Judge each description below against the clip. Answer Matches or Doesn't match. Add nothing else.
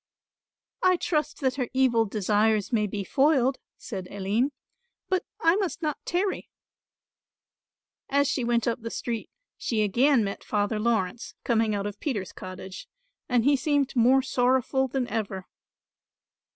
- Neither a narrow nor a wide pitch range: Matches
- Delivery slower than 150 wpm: Matches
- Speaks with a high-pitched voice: Matches